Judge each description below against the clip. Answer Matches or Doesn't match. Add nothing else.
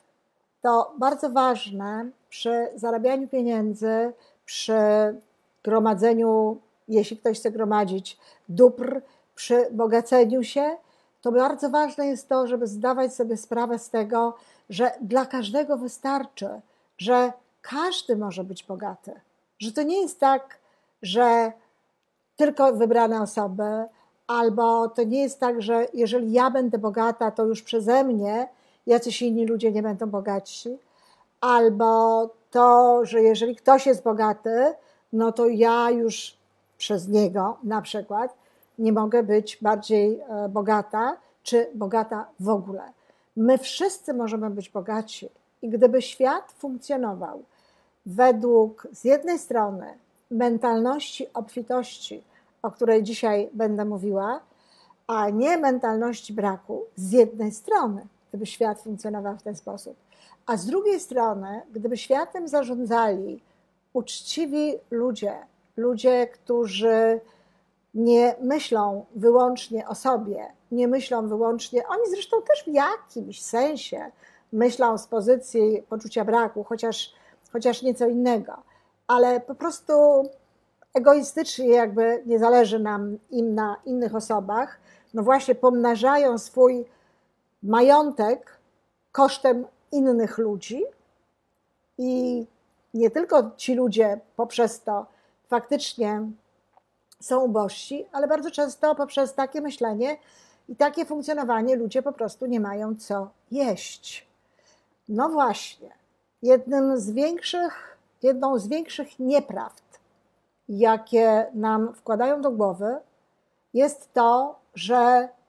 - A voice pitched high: Matches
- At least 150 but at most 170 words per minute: Doesn't match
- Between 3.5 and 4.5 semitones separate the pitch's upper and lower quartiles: Doesn't match